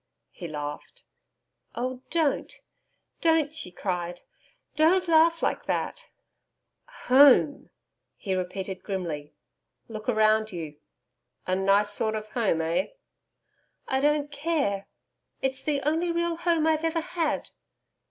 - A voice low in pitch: No, very high, 255 Hz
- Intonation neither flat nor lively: No, wide, 8.8 semitones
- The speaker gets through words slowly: Yes, slow, 115 wpm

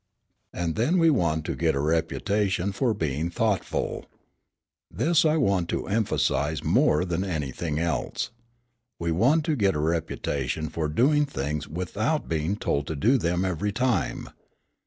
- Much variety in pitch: Yes, wide, 6.2 semitones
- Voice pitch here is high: No, very low, 90 Hz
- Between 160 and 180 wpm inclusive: No, average, 150 wpm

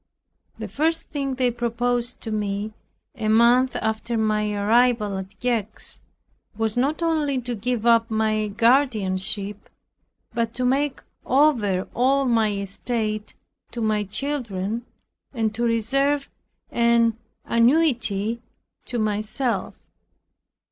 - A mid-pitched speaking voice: No, high, 230 Hz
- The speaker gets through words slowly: Yes, slow, 115 wpm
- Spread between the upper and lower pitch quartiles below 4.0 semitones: Yes, average, 2.8 semitones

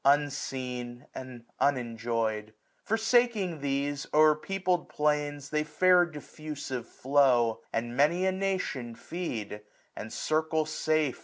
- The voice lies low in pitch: No, medium, 145 Hz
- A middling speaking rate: No, slow, 120 wpm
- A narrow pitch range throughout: No, average, 4.4 semitones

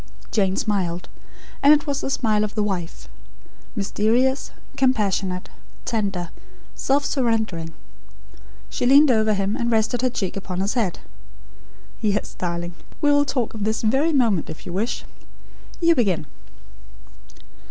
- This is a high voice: Yes, high, 215 Hz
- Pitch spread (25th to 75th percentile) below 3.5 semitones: No, average, 4.9 semitones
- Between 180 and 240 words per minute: No, slow, 135 wpm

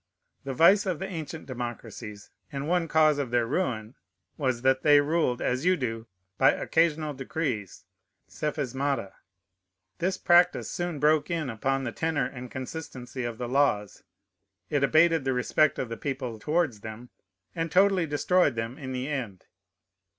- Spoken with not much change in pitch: No, average, 4.7 semitones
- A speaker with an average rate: Yes, average, 155 wpm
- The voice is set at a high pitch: No, medium, 140 Hz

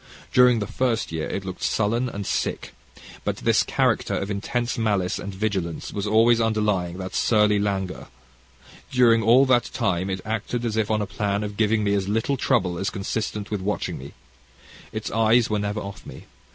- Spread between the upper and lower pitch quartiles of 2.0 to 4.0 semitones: Yes, narrow, 2.4 semitones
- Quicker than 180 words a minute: Yes, average, 190 wpm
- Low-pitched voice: Yes, low, 105 Hz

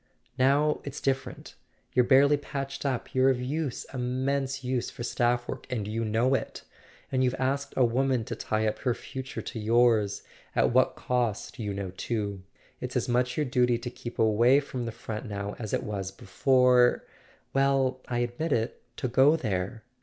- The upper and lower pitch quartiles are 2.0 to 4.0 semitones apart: Yes, average, 2.9 semitones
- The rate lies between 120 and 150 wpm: No, average, 175 wpm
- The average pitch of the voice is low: Yes, low, 125 Hz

